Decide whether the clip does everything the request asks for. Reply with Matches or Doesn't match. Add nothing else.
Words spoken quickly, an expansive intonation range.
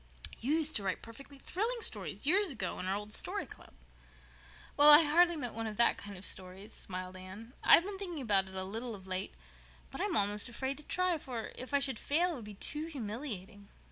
Matches